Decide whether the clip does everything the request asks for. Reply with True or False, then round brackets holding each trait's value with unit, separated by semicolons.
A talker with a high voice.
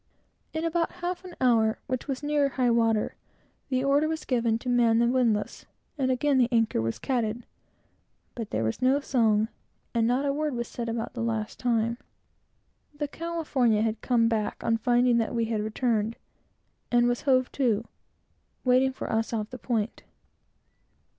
True (240 Hz)